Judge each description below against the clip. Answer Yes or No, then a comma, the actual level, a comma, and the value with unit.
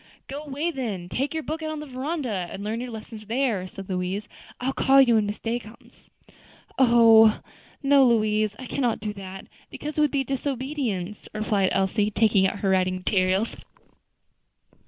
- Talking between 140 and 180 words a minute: Yes, average, 175 wpm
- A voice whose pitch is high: Yes, high, 225 Hz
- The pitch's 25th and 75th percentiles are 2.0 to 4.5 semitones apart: No, average, 5.2 semitones